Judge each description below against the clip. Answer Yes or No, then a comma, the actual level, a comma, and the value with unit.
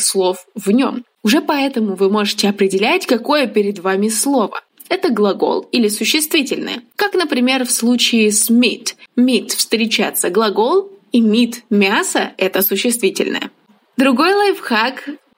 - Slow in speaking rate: Yes, slow, 130 wpm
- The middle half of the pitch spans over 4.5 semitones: Yes, average, 5.2 semitones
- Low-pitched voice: No, high, 240 Hz